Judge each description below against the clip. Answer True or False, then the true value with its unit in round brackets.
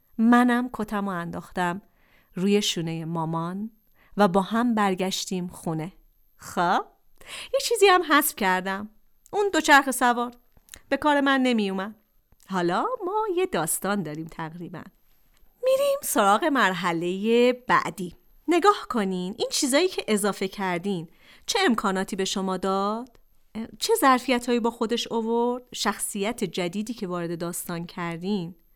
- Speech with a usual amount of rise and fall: True (5.0 semitones)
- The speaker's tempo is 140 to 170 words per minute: False (125 wpm)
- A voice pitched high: True (205 Hz)